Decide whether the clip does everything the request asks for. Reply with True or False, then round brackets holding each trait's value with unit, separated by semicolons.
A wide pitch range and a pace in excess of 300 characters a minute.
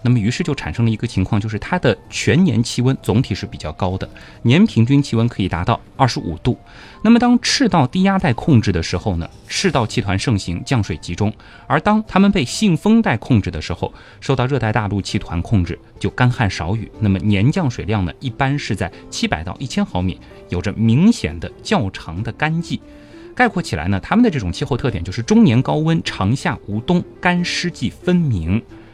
True (6.8 semitones; 310 characters per minute)